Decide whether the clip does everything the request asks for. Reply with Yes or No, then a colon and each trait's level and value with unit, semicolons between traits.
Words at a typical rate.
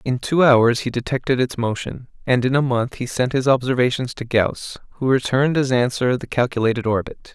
Yes: average, 195 wpm